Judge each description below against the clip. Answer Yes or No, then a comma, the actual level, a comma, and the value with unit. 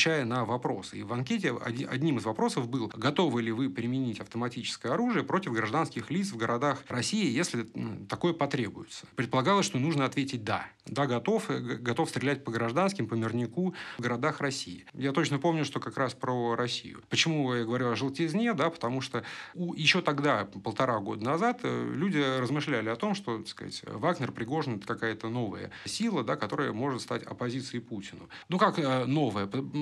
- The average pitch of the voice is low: Yes, low, 130 Hz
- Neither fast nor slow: No, fast, 165 wpm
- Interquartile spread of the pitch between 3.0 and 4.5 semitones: No, average, 5.0 semitones